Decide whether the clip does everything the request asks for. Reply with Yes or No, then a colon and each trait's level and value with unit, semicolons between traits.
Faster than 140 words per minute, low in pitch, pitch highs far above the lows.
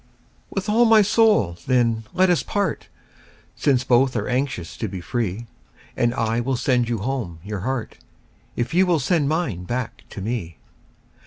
Yes: average, 170 wpm; low, 125 Hz; wide, 6.0 semitones